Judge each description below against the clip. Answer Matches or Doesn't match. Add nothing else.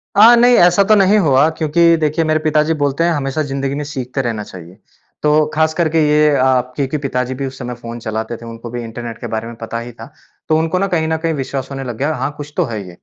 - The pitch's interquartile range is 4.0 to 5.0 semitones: Matches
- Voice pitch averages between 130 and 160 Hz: Matches